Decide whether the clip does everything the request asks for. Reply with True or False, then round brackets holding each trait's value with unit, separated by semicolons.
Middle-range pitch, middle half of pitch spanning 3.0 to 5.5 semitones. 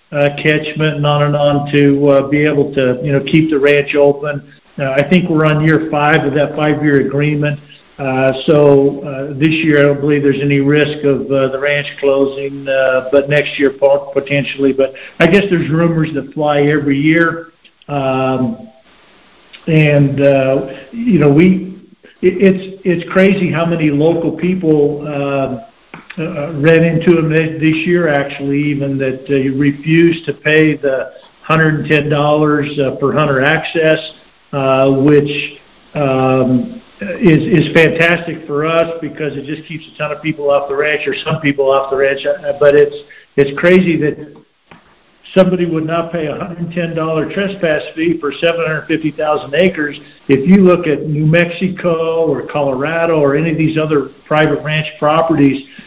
False (150 Hz; 2.4 semitones)